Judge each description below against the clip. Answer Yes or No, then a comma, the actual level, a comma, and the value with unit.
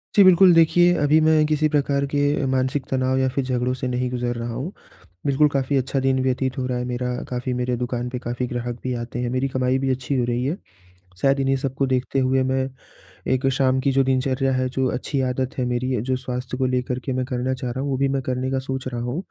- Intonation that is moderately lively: No, narrow, 1.4 semitones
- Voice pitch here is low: Yes, low, 130 Hz